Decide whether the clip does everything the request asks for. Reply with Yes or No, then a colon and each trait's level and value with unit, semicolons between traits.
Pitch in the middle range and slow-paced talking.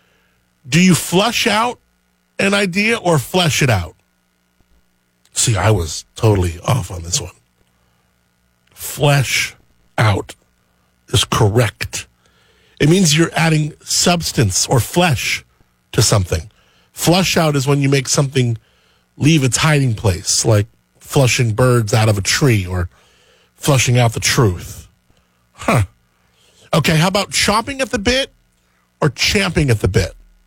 No: low, 110 Hz; slow, 130 wpm